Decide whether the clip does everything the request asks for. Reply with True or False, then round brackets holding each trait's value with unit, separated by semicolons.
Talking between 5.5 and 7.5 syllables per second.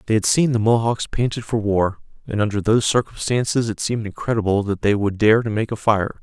True (6.0 syllables/s)